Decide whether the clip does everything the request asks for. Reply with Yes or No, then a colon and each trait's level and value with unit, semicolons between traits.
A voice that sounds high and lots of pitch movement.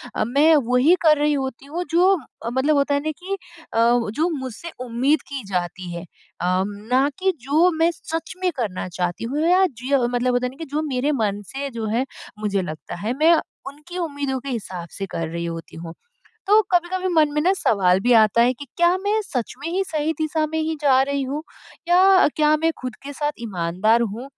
Yes: very high, 275 Hz; wide, 5.7 semitones